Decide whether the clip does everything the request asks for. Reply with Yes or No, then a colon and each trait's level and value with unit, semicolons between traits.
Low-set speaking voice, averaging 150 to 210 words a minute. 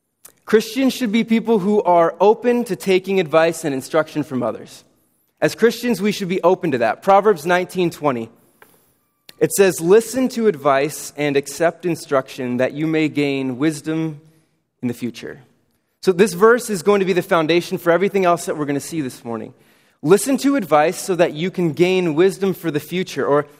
No: medium, 175 Hz; average, 185 wpm